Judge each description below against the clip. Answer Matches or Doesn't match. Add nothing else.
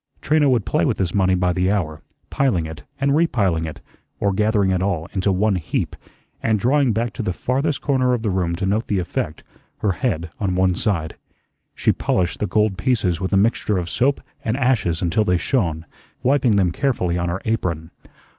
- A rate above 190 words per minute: Matches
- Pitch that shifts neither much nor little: Matches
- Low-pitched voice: Matches